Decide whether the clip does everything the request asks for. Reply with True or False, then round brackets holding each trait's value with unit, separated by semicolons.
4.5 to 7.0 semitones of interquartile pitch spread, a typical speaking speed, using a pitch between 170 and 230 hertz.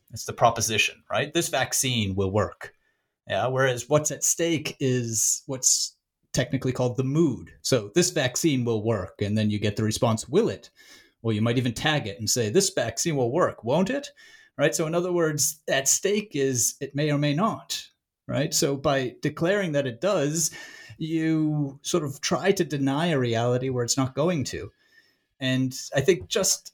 False (5.2 semitones; 185 wpm; 140 Hz)